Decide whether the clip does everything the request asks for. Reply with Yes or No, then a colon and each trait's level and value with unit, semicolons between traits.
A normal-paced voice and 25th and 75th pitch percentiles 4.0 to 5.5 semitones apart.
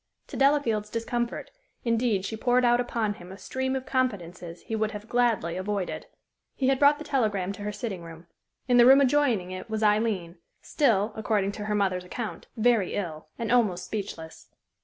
Yes: average, 180 wpm; average, 4.3 semitones